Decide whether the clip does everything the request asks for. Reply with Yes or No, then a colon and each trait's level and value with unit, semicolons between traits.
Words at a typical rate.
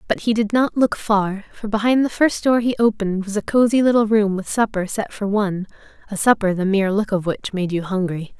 No: fast, 235 wpm